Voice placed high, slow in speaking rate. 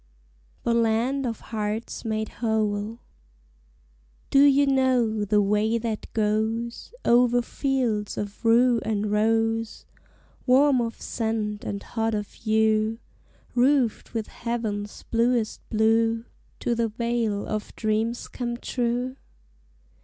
Yes: high, 225 Hz; slow, 115 wpm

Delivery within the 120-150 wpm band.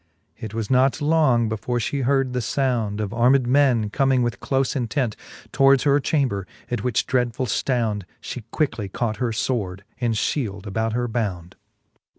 No: average, 165 wpm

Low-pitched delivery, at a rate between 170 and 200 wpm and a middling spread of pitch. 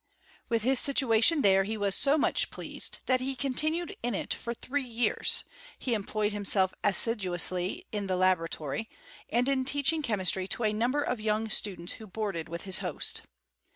No: high, 220 Hz; average, 180 wpm; average, 4.9 semitones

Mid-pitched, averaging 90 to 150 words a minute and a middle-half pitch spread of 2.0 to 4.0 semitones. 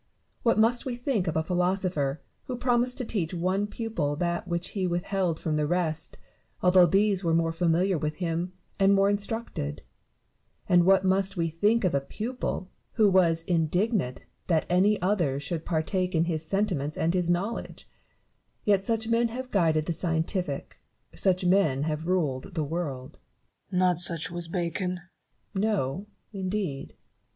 No: medium, 180 Hz; average, 165 wpm; average, 3.4 semitones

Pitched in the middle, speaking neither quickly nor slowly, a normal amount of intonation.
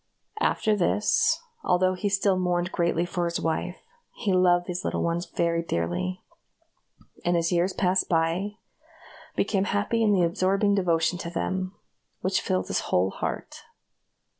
No: medium, 180 Hz; average, 145 wpm; narrow, 2.3 semitones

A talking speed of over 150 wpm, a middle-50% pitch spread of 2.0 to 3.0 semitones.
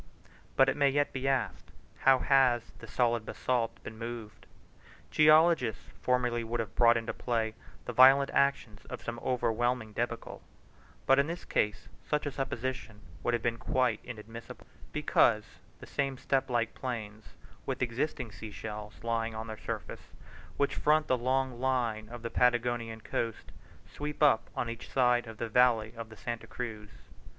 Yes: average, 160 wpm; narrow, 2.6 semitones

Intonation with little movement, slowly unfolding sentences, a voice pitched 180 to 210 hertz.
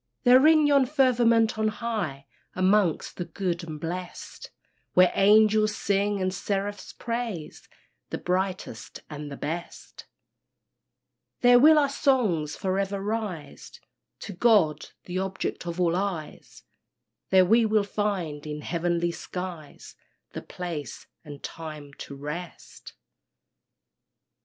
No: average, 4.5 semitones; slow, 120 wpm; medium, 185 Hz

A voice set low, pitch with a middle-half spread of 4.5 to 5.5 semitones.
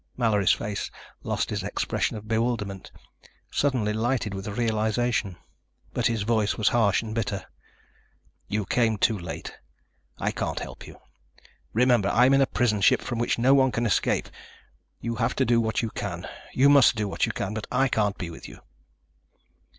No: low, 110 Hz; average, 2.7 semitones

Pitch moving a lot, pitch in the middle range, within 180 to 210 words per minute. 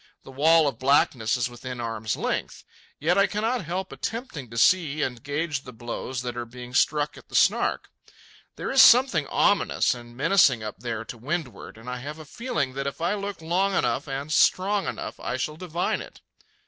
Yes: wide, 6.1 semitones; medium, 145 Hz; average, 195 wpm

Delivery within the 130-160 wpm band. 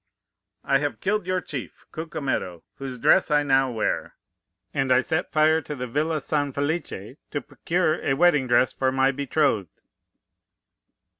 Yes: average, 150 wpm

